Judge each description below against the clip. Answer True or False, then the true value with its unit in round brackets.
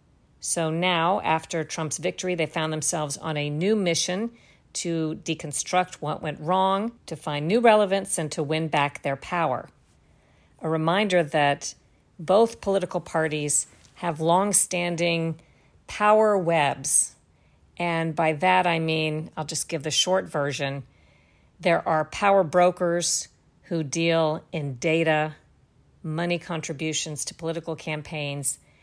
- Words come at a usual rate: False (130 wpm)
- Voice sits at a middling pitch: True (160 Hz)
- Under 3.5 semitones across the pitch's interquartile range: True (2.6 semitones)